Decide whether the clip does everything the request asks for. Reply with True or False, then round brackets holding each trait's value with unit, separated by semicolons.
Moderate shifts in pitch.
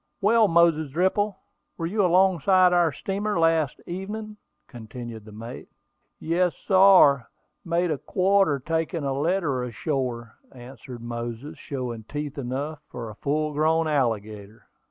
False (6.4 semitones)